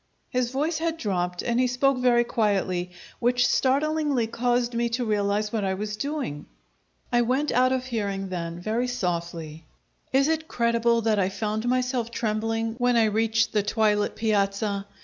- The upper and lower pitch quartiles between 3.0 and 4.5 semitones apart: Yes, average, 3.5 semitones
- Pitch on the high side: Yes, high, 230 Hz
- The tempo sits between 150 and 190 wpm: Yes, average, 165 wpm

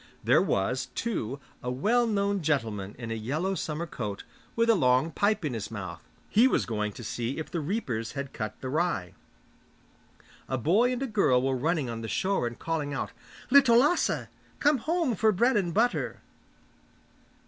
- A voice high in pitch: No, medium, 155 Hz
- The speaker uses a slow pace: No, average, 180 wpm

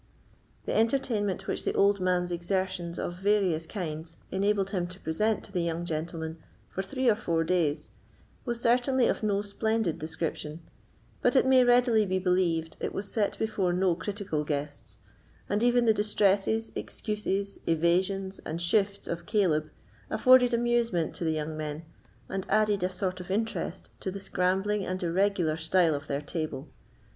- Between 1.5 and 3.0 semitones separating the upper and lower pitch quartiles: No, average, 4.1 semitones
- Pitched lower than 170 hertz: No, high, 190 Hz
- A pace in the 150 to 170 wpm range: Yes, average, 160 wpm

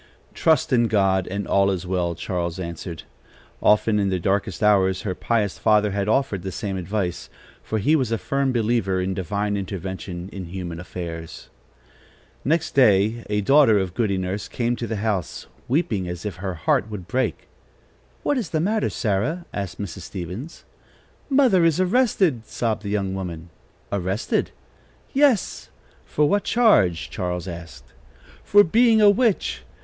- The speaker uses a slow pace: No, average, 155 wpm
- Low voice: Yes, low, 100 Hz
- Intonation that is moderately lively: No, wide, 6.0 semitones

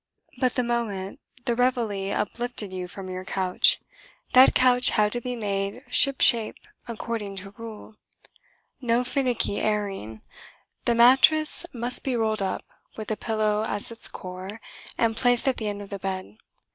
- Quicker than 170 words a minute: No, average, 160 wpm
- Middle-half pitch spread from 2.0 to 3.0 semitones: No, average, 3.7 semitones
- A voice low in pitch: No, high, 220 Hz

